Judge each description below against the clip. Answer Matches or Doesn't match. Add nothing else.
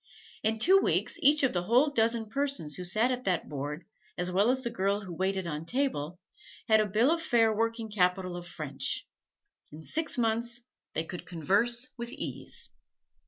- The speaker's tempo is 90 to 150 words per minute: Doesn't match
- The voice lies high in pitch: Matches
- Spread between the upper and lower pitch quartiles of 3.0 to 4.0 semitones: Doesn't match